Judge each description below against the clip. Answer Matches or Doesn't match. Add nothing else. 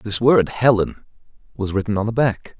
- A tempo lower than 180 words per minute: Matches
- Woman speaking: Doesn't match